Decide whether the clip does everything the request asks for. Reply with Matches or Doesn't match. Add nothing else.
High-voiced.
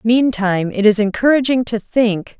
Matches